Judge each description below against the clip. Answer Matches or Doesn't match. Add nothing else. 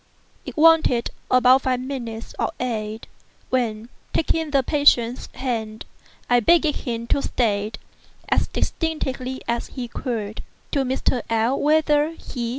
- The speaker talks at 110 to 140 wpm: Matches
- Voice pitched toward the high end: Matches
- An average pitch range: Matches